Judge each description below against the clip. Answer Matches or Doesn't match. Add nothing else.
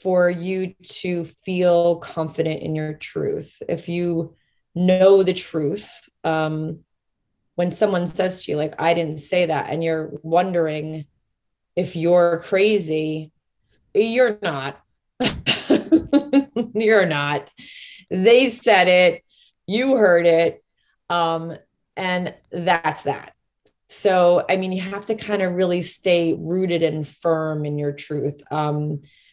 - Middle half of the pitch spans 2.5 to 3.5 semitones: Matches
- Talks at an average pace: Doesn't match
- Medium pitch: Matches